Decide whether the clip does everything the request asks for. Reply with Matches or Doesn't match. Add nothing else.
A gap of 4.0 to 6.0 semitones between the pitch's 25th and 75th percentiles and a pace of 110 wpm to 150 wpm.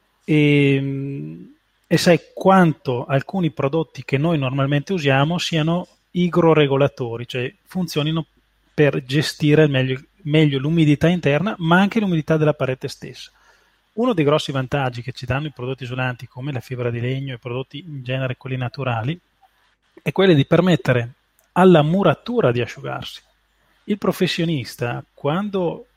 Matches